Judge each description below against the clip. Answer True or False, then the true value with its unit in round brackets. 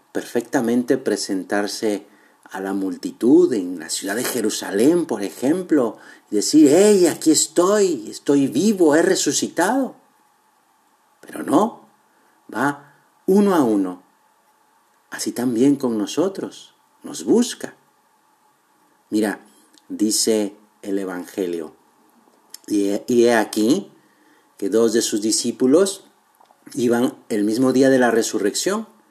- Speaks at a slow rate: True (105 wpm)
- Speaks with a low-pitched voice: True (130 Hz)